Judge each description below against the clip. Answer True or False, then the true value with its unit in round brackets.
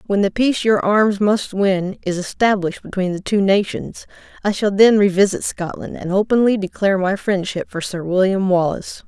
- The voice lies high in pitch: True (200 Hz)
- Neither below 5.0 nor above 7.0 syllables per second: True (5.2 syllables/s)